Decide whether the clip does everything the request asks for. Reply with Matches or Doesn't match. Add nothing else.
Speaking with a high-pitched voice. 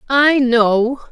Matches